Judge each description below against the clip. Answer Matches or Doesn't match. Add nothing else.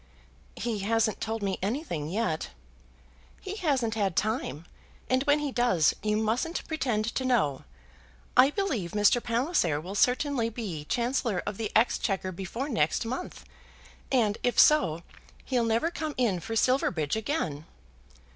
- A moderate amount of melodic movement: Matches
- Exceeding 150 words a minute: Doesn't match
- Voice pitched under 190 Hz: Doesn't match